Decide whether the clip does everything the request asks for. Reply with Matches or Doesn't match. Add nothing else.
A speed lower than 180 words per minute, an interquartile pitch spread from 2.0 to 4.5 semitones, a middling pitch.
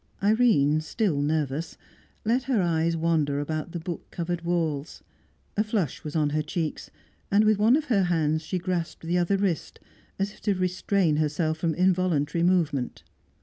Matches